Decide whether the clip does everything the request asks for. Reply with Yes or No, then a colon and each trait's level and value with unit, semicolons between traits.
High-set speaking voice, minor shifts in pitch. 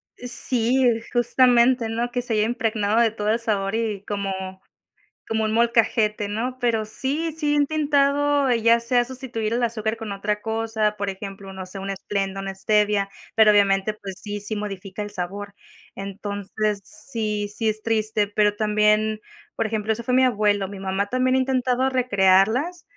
No: high, 220 Hz; average, 3.0 semitones